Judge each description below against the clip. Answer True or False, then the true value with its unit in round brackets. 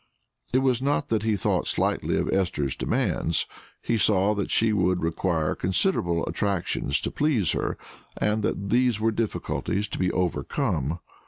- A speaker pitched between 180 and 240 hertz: False (100 Hz)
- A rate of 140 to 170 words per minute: True (155 wpm)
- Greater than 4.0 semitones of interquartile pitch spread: True (4.4 semitones)